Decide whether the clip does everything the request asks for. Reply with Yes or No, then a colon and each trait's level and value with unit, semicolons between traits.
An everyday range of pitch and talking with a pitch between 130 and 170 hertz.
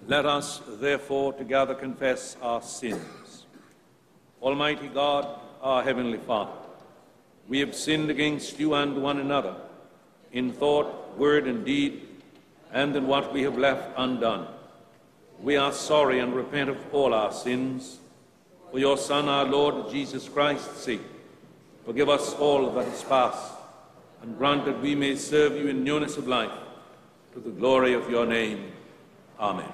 No: narrow, 2.0 semitones; medium, 140 Hz